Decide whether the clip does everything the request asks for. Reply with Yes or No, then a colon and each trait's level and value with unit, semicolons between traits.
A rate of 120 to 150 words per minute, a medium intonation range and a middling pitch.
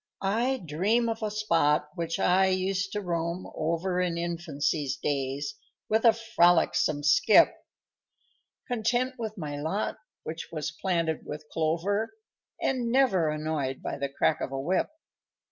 No: average, 140 wpm; wide, 5.7 semitones; medium, 170 Hz